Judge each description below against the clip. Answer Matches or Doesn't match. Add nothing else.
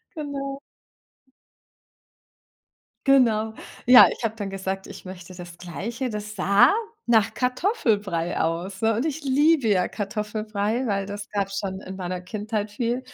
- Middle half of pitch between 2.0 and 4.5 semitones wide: Matches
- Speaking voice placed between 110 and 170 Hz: Doesn't match